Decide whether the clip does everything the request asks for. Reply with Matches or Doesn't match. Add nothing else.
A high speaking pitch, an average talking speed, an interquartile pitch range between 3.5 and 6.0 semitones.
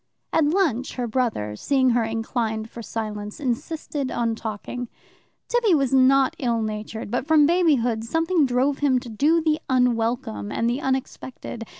Matches